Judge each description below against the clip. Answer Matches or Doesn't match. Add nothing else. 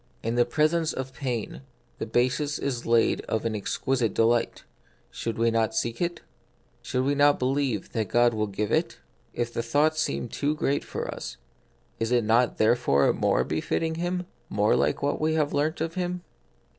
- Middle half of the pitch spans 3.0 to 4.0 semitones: Doesn't match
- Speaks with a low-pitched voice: Matches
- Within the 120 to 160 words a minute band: Doesn't match